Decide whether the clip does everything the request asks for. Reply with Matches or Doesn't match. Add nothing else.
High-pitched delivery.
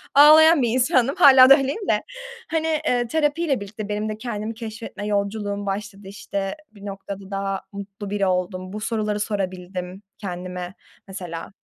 Matches